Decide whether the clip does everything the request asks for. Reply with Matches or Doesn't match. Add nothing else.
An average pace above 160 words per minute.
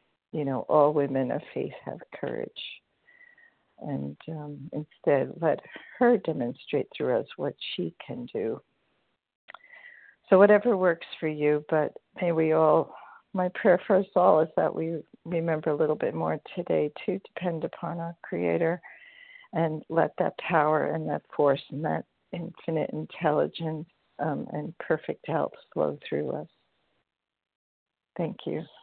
Doesn't match